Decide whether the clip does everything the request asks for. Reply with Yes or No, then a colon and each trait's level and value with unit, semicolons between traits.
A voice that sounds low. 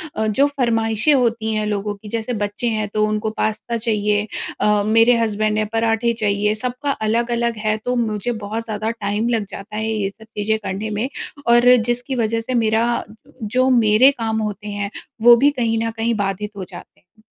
No: high, 220 Hz